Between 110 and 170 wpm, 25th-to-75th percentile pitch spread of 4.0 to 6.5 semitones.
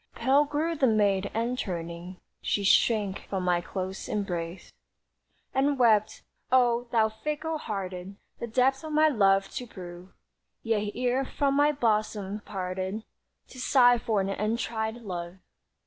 Yes: average, 140 wpm; average, 4.7 semitones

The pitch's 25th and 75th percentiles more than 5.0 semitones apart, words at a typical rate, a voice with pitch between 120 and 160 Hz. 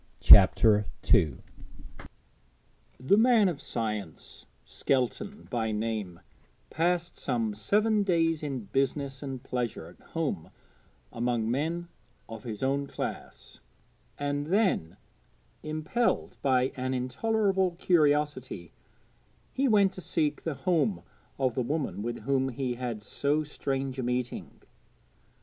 No: wide, 5.6 semitones; slow, 115 wpm; low, 135 Hz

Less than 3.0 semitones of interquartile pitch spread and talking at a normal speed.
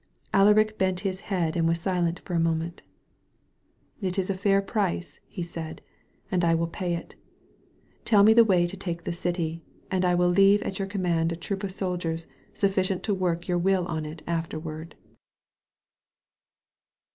Yes: narrow, 2.6 semitones; average, 170 wpm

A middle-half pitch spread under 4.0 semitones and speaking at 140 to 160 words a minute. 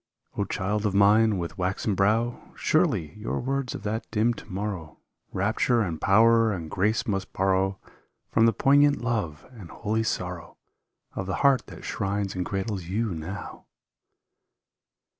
Yes: average, 3.1 semitones; average, 150 wpm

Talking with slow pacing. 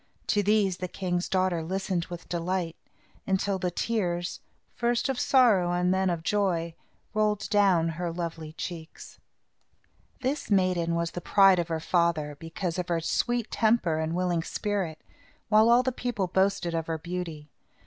No: average, 160 wpm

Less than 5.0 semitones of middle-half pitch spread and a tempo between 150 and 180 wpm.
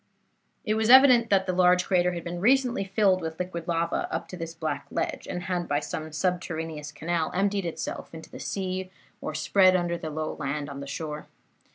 No: average, 3.0 semitones; average, 200 wpm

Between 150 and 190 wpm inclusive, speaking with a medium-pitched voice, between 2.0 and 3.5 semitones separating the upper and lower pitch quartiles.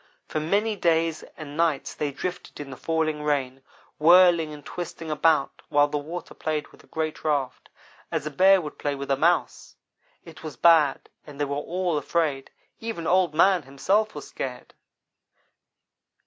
Yes: average, 165 wpm; medium, 155 Hz; average, 2.9 semitones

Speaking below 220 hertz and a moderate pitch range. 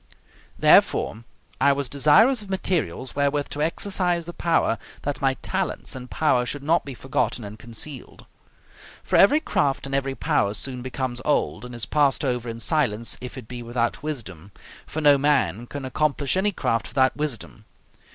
Yes: low, 135 Hz; average, 3.8 semitones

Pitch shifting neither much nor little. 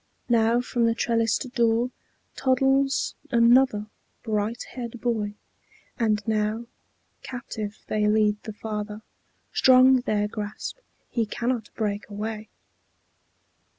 No: narrow, 2.3 semitones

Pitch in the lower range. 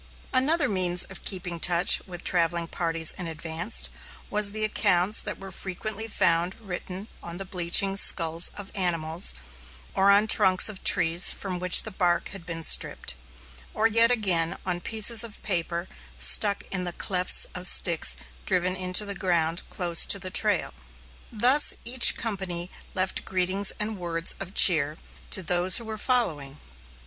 No: medium, 185 Hz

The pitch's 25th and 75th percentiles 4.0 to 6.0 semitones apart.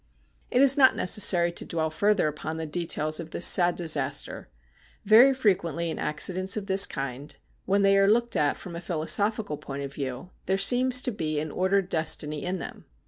Yes: average, 4.5 semitones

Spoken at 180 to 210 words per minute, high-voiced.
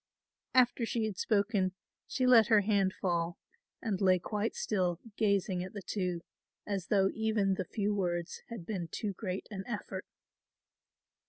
No: average, 155 wpm; high, 200 Hz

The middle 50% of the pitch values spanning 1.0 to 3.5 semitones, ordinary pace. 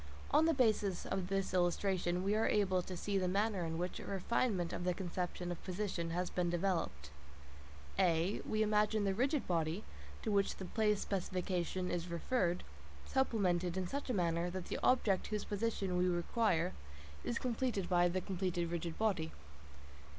Yes: average, 3.1 semitones; average, 170 wpm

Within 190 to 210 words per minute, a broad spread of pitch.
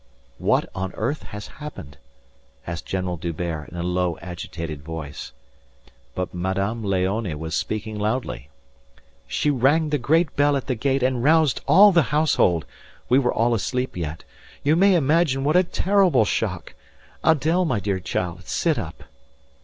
No: average, 155 wpm; wide, 8.8 semitones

